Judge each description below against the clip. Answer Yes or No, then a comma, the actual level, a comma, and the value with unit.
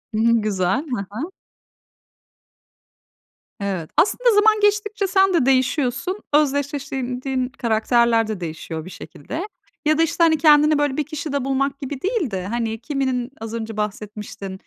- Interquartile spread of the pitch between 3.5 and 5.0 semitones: No, wide, 5.6 semitones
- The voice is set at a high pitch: Yes, very high, 265 Hz